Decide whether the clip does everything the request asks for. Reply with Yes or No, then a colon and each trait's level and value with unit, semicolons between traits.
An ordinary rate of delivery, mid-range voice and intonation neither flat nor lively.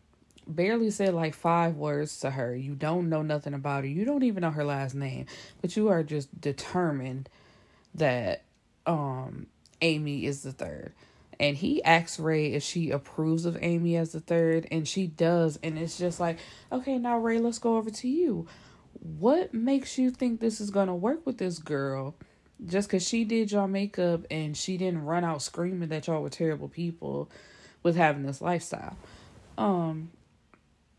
Yes: average, 175 wpm; medium, 165 Hz; average, 4.7 semitones